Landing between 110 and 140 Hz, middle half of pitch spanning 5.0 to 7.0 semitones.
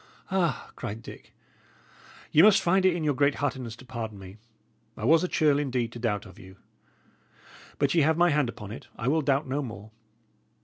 Yes: low, 135 Hz; wide, 5.6 semitones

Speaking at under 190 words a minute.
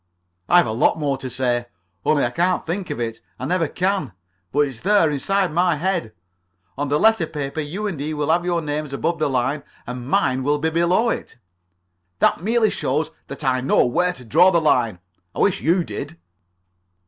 No: average, 195 wpm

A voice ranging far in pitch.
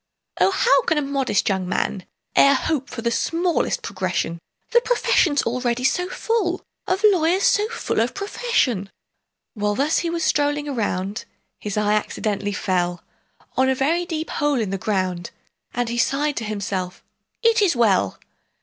Yes: wide, 8.6 semitones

